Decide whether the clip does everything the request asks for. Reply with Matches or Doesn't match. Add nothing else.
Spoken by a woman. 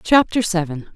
Matches